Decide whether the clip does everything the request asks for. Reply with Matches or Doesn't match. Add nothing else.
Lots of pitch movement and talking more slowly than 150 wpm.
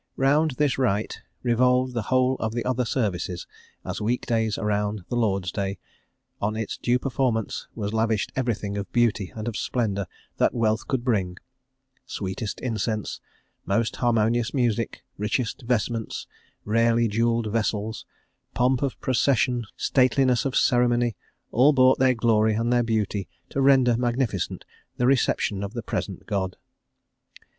Doesn't match